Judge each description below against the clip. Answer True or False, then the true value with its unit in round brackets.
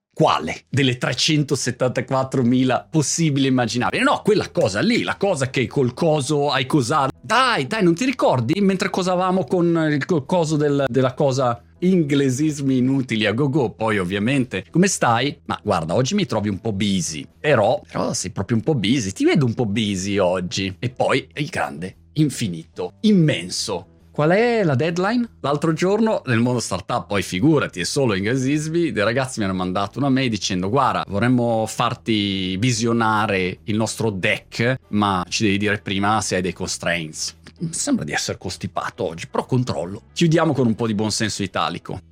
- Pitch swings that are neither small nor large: False (6.7 semitones)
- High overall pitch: False (130 Hz)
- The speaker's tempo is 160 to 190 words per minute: True (170 wpm)